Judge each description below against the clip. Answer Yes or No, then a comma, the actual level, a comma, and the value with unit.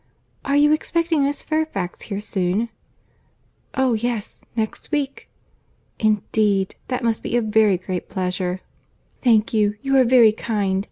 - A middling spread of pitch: Yes, average, 4.9 semitones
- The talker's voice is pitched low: No, high, 220 Hz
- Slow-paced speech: Yes, slow, 130 wpm